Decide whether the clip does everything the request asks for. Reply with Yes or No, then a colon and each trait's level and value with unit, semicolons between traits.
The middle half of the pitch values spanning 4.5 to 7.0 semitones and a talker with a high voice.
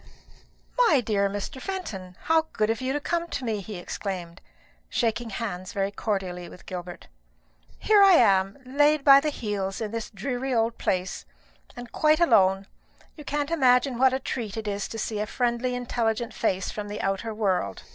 Yes: average, 5.1 semitones; high, 225 Hz